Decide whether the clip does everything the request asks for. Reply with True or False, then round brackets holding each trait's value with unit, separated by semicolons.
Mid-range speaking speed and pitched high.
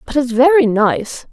True (180 wpm; 260 Hz)